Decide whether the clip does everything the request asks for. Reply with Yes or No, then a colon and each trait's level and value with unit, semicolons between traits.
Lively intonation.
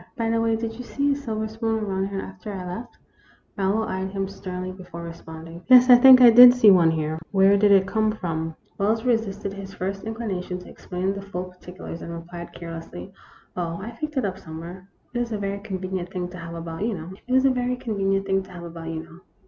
No: average, 3.9 semitones